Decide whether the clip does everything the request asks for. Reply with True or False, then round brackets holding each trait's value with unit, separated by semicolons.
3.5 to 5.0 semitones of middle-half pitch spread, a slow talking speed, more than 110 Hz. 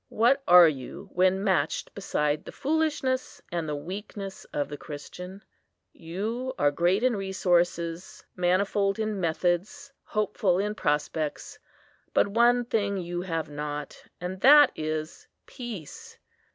True (4.5 semitones; 125 wpm; 185 Hz)